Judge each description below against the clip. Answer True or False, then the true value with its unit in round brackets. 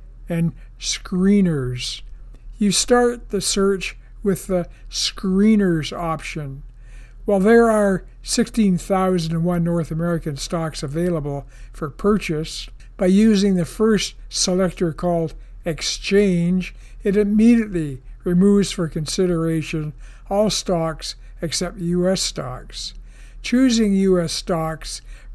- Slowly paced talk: True (95 wpm)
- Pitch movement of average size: True (4.5 semitones)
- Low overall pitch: False (175 Hz)